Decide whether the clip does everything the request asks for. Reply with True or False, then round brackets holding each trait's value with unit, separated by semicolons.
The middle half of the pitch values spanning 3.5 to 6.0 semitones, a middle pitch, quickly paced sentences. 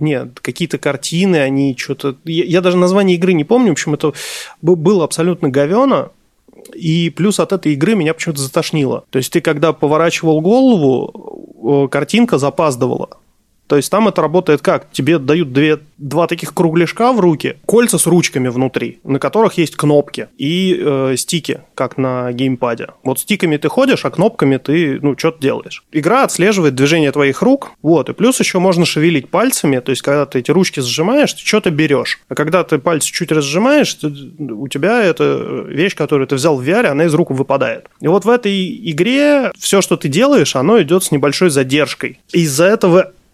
True (4.6 semitones; 165 Hz; 180 wpm)